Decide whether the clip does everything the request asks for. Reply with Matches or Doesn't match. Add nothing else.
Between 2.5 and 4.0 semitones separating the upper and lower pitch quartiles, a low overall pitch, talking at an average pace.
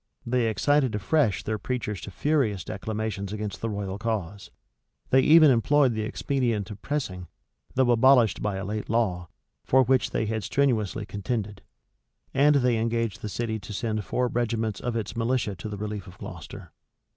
Matches